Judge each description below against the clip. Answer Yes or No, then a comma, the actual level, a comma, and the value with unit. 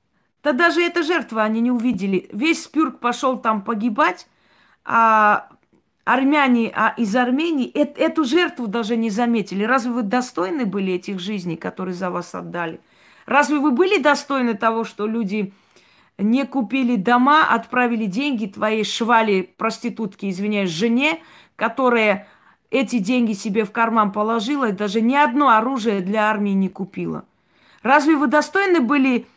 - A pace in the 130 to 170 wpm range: Yes, average, 140 wpm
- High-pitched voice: Yes, high, 235 Hz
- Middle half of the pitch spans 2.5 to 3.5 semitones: No, average, 4.1 semitones